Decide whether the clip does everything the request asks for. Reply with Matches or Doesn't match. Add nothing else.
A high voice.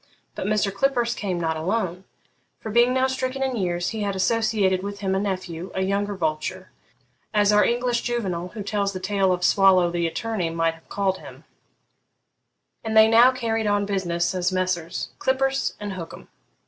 Matches